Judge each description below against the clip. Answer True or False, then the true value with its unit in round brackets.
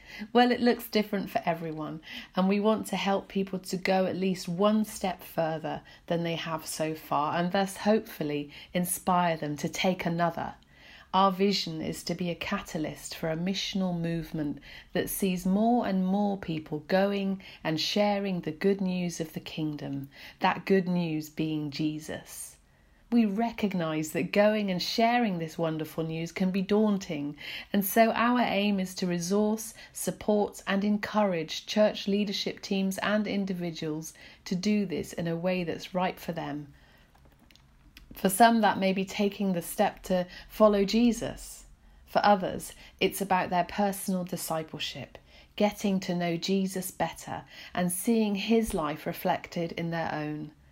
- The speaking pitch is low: False (185 Hz)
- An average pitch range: True (3.7 semitones)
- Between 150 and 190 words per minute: True (155 wpm)